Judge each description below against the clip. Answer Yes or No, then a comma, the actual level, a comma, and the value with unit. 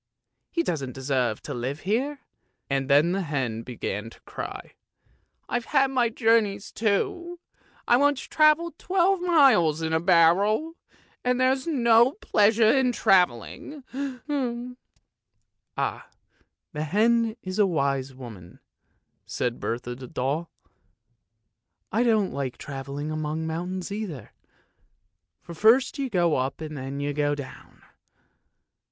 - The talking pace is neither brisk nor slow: No, slow, 130 wpm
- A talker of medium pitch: Yes, medium, 180 Hz